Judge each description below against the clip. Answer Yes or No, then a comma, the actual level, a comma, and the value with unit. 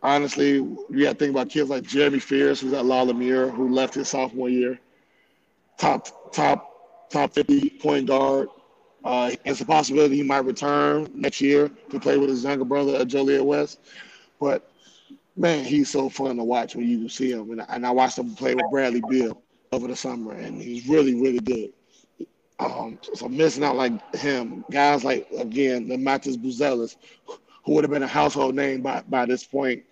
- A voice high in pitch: No, low, 135 Hz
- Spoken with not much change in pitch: Yes, narrow, 2.0 semitones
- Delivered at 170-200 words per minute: Yes, average, 190 wpm